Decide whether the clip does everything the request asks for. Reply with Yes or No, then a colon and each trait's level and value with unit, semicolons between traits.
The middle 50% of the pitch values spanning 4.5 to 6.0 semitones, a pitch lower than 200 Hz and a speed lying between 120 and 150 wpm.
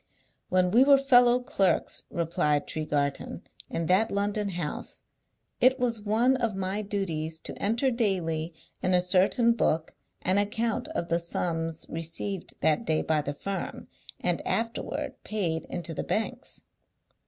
Yes: wide, 5.5 semitones; high, 190 Hz; average, 140 wpm